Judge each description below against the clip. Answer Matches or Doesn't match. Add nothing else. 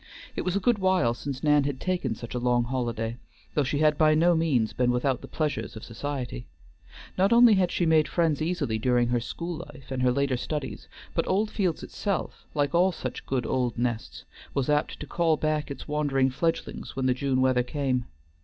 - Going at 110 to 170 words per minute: Doesn't match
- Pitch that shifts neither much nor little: Matches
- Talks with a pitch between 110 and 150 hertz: Matches